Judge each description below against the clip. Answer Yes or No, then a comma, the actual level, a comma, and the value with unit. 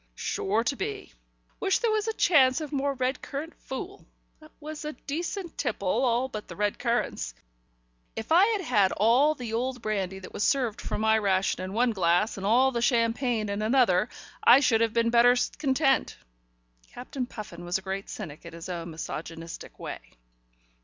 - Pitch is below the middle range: No, high, 235 Hz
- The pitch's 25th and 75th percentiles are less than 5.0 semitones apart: No, wide, 5.4 semitones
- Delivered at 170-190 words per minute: Yes, average, 180 wpm